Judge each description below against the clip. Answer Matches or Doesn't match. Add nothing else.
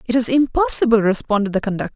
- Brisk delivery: Doesn't match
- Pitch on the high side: Matches